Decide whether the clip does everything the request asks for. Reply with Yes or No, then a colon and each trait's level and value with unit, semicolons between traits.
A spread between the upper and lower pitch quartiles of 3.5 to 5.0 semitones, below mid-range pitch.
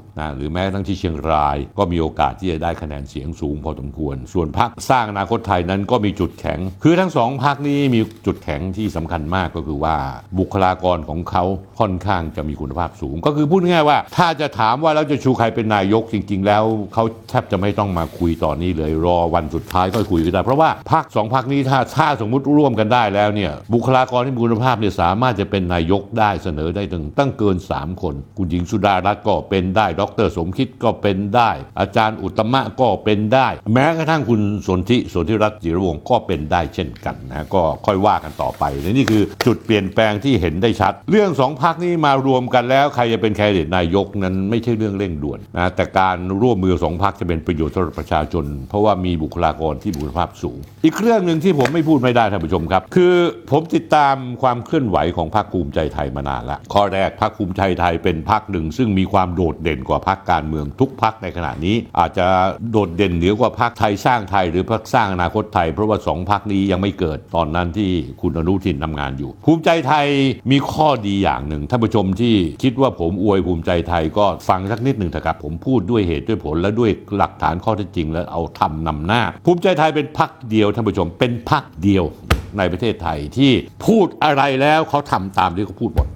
No: wide, 5.4 semitones; low, 100 Hz